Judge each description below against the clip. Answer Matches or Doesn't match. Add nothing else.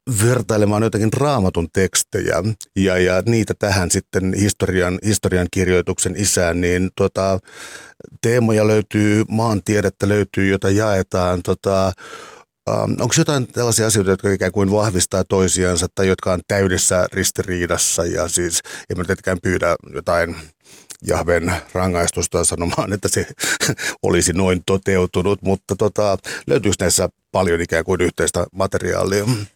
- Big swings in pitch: Doesn't match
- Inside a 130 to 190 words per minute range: Doesn't match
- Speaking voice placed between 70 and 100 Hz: Matches